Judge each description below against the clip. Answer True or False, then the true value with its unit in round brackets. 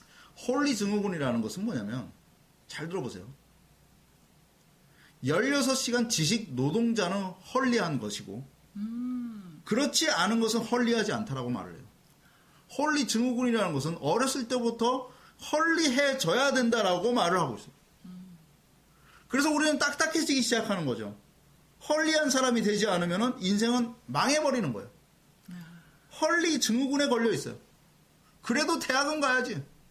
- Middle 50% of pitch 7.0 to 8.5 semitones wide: True (7.3 semitones)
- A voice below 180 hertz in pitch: False (230 Hz)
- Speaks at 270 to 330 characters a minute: True (285 characters per minute)